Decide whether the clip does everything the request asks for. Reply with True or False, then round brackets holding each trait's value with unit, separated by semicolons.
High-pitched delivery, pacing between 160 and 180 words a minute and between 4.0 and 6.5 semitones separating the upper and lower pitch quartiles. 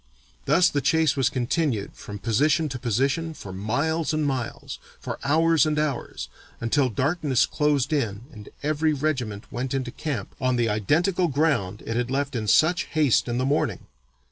False (140 Hz; 170 wpm; 4.5 semitones)